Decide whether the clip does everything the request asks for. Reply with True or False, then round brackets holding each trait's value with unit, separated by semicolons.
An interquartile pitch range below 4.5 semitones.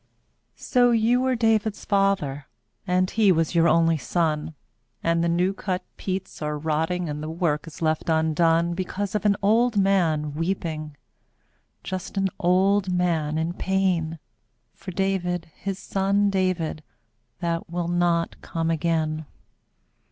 True (3.2 semitones)